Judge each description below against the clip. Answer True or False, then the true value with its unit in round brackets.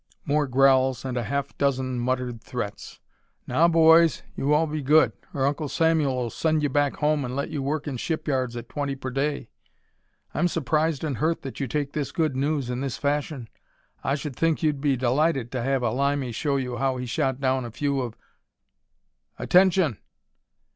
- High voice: False (140 Hz)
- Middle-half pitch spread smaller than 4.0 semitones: True (2.8 semitones)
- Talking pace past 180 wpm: True (190 wpm)